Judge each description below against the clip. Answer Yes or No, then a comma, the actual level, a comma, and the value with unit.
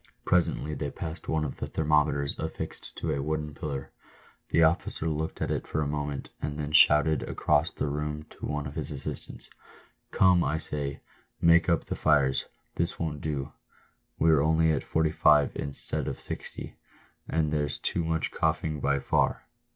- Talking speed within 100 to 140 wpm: No, average, 170 wpm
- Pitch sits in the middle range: No, very low, 75 Hz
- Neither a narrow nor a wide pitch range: No, narrow, 1.6 semitones